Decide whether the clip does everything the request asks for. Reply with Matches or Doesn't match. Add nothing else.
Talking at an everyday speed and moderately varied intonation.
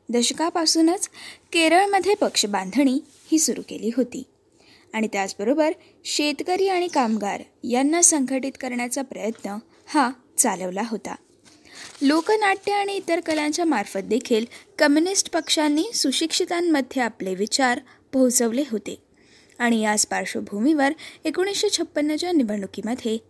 Doesn't match